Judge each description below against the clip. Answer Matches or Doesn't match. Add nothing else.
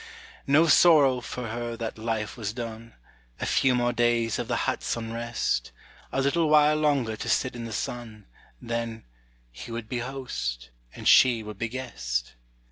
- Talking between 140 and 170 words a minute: Matches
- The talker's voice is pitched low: Matches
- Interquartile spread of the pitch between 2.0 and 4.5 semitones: Matches